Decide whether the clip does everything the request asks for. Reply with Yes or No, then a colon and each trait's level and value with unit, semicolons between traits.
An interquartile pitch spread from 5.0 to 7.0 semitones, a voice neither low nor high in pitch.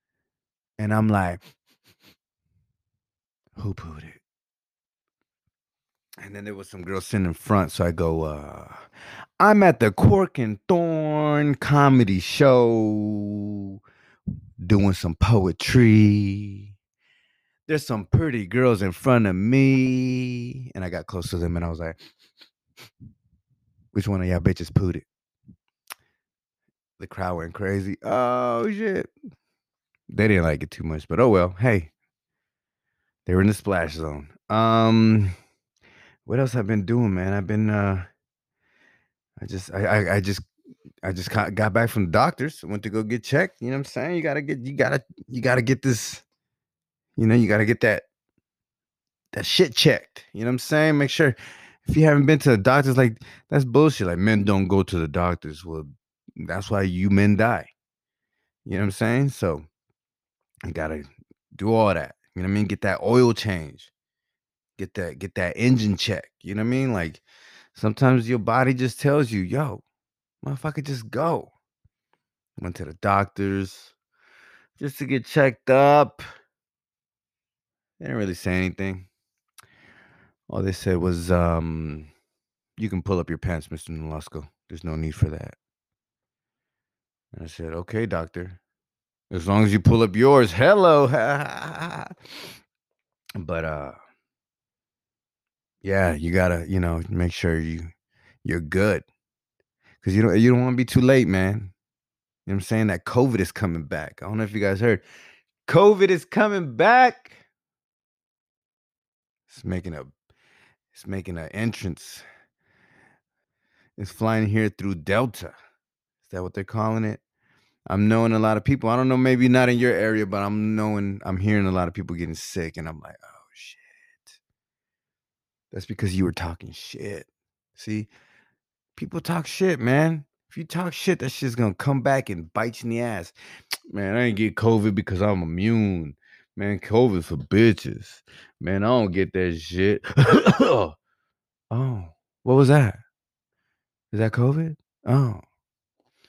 No: average, 5.3 semitones; low, 105 Hz